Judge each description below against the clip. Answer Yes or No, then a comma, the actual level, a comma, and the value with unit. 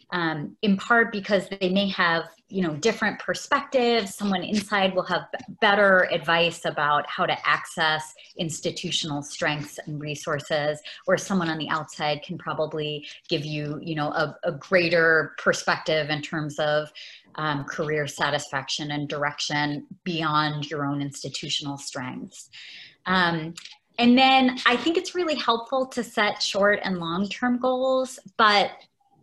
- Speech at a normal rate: Yes, average, 145 wpm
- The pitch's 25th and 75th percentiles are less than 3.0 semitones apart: No, average, 5.3 semitones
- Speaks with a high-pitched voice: No, medium, 170 Hz